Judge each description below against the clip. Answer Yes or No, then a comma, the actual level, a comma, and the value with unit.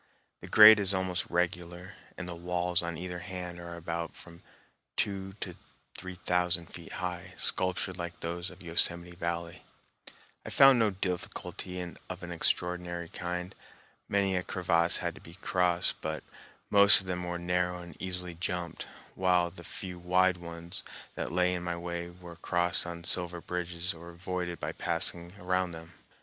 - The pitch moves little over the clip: Yes, narrow, 1.1 semitones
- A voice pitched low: Yes, very low, 90 Hz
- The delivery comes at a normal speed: Yes, average, 160 wpm